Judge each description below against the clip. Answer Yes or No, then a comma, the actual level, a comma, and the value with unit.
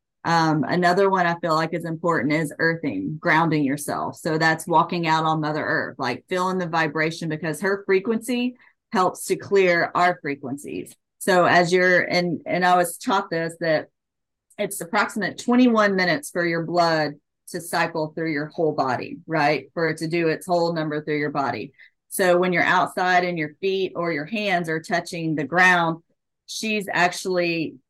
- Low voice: No, medium, 170 Hz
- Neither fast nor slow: Yes, average, 175 wpm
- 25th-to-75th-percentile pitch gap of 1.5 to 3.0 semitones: Yes, narrow, 2.4 semitones